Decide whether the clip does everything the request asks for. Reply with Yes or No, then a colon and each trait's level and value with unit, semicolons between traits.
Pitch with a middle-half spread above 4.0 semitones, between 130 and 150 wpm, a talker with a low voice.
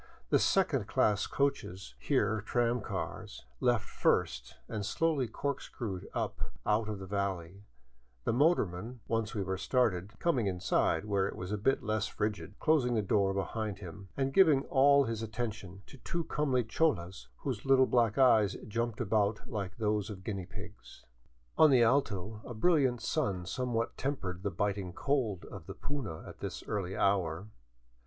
No: average, 4.5 semitones; average, 160 wpm; low, 110 Hz